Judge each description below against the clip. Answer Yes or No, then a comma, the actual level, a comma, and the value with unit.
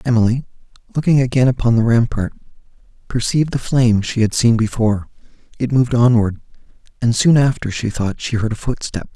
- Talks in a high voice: No, low, 120 Hz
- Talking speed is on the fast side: No, average, 165 wpm